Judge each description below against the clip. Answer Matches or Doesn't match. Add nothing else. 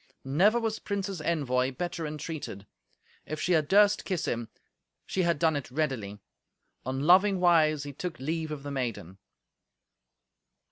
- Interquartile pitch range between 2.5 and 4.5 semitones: Doesn't match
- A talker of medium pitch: Matches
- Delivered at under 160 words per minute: Matches